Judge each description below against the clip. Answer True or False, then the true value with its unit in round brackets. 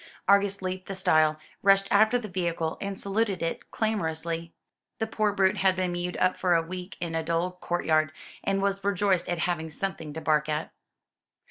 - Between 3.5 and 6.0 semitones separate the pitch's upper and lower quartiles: False (3.0 semitones)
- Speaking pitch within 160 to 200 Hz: True (185 Hz)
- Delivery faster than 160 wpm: True (185 wpm)